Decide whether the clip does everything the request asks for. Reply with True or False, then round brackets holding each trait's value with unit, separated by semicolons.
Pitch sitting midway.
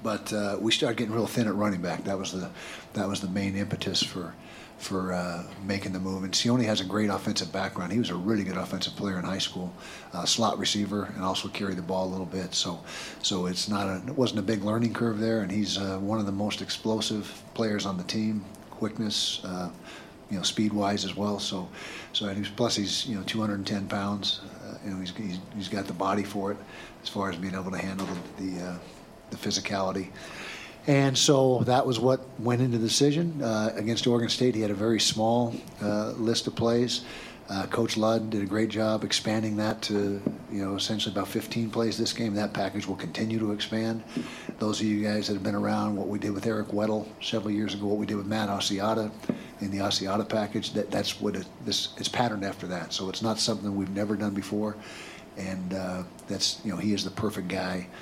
False (105 Hz)